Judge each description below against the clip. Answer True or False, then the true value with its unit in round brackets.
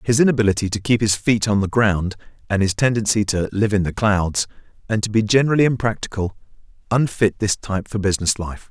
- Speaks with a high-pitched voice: False (105 Hz)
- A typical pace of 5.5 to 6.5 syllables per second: True (6.0 syllables/s)